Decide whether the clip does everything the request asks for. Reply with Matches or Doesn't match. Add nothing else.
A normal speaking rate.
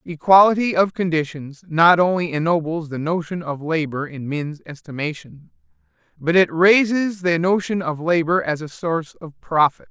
Matches